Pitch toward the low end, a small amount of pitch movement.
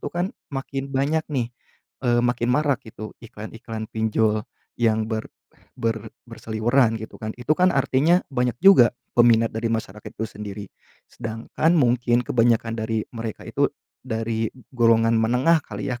Yes: low, 115 Hz; narrow, 2.3 semitones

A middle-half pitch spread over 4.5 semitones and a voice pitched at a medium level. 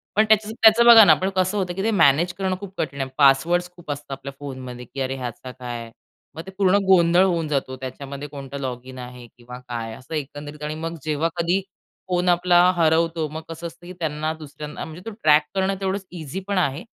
Yes: average, 5.0 semitones; medium, 155 Hz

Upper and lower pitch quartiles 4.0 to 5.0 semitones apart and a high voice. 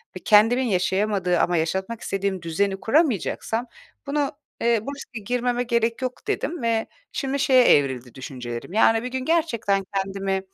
Yes: average, 4.6 semitones; high, 220 Hz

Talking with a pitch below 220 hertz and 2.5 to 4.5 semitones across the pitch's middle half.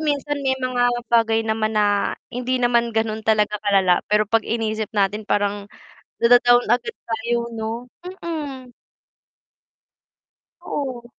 No: high, 230 Hz; average, 2.8 semitones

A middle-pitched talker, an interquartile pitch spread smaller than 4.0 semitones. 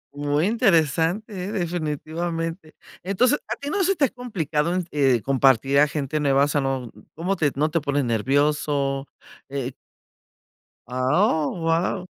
No: medium, 155 Hz; average, 4.4 semitones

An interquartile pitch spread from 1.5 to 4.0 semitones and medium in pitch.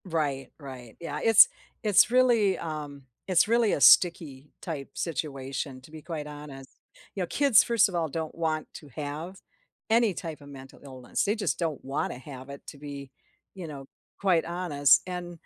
No: average, 4.7 semitones; medium, 155 Hz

